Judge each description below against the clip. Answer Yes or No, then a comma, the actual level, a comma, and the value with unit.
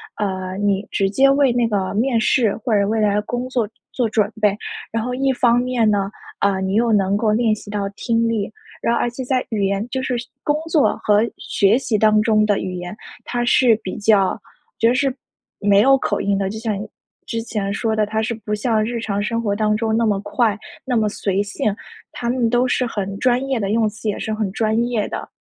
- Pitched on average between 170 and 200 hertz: No, high, 220 Hz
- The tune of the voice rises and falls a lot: No, average, 2.9 semitones